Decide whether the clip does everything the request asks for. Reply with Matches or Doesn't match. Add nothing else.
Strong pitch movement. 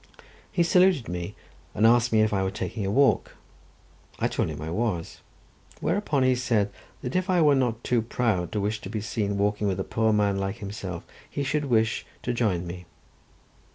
Doesn't match